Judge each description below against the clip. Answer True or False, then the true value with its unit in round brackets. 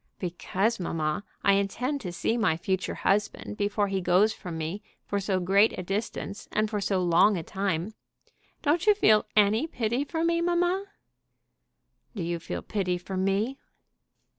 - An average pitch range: True (3.6 semitones)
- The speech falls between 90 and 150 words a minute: False (165 wpm)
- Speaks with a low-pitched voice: False (200 Hz)